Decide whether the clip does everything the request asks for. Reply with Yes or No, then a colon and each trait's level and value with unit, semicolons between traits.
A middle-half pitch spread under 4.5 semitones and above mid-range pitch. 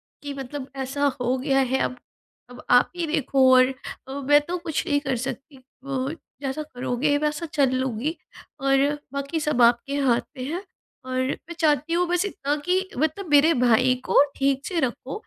Yes: average, 2.9 semitones; very high, 280 Hz